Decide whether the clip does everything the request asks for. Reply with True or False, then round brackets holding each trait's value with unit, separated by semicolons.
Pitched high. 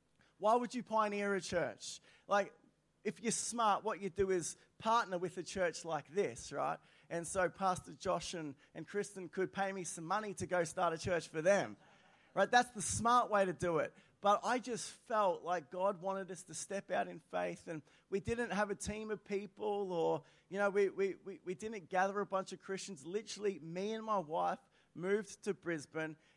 True (195 Hz)